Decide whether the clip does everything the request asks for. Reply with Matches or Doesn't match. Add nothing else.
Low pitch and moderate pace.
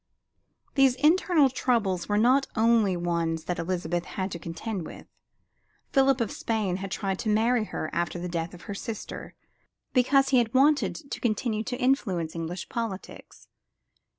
Doesn't match